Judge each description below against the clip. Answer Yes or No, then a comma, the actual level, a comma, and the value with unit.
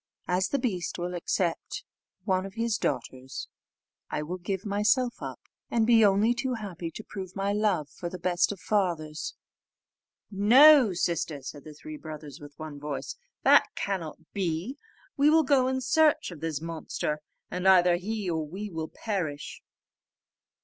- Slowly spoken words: No, average, 165 wpm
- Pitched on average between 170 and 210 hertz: Yes, medium, 185 Hz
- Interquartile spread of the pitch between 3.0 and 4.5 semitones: No, average, 5.1 semitones